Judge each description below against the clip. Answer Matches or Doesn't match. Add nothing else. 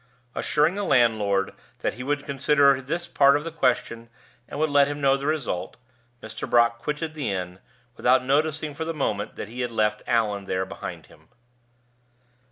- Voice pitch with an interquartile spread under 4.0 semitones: Doesn't match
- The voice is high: Doesn't match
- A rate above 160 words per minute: Matches